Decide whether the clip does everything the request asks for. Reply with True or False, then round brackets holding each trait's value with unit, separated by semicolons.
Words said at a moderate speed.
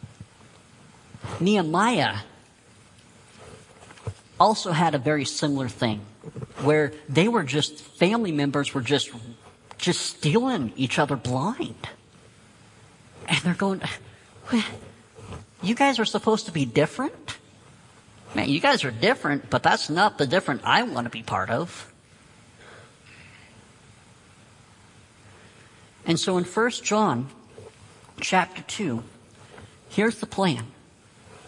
False (105 wpm)